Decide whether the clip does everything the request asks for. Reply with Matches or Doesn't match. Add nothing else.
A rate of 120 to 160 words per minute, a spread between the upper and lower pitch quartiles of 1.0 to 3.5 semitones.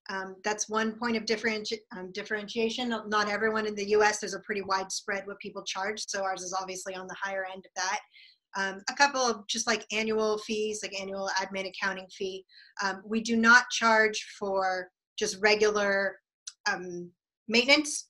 Doesn't match